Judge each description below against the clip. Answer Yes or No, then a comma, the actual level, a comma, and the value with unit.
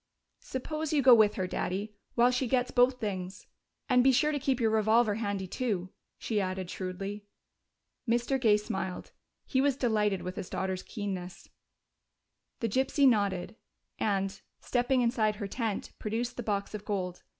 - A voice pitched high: Yes, high, 215 Hz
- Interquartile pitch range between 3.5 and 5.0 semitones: Yes, average, 4.2 semitones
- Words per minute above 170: No, average, 160 wpm